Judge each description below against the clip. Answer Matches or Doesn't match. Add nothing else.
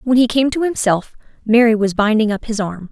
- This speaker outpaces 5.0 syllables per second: Matches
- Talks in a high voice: Matches